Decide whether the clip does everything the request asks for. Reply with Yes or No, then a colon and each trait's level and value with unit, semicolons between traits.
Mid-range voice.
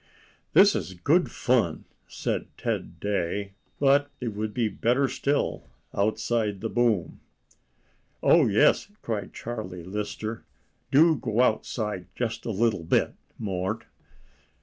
No: low, 110 Hz